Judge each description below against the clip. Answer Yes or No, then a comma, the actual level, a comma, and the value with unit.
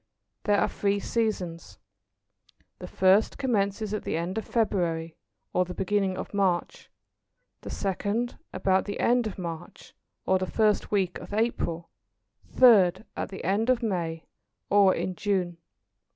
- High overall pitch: Yes, high, 195 Hz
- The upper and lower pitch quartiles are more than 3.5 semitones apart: No, average, 3.0 semitones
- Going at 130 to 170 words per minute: Yes, average, 145 wpm